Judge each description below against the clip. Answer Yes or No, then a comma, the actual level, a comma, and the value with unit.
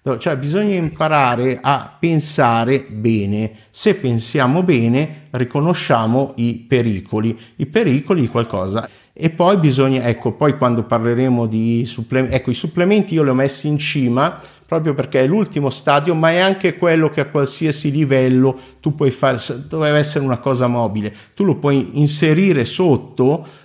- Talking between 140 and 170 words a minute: Yes, average, 150 wpm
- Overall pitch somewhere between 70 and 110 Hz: No, low, 135 Hz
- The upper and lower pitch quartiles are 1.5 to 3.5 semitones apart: No, average, 4.2 semitones